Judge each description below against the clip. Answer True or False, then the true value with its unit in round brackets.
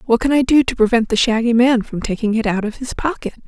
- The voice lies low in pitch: False (235 Hz)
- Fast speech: True (275 wpm)